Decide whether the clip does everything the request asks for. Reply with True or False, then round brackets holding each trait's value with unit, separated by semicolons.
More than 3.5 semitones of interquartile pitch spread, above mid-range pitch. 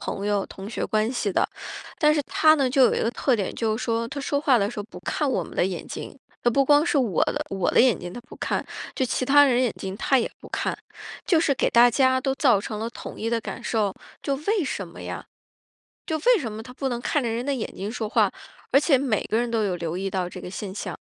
True (4.8 semitones; 240 Hz)